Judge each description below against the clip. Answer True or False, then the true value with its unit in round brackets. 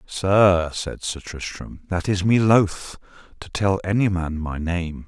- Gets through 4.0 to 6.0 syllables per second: False (3.7 syllables/s)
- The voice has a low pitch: True (90 Hz)